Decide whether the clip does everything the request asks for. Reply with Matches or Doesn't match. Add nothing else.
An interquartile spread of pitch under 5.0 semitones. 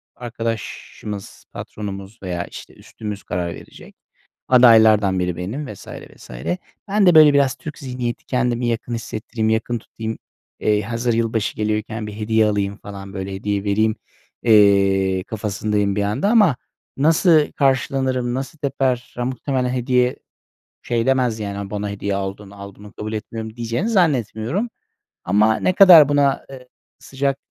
Matches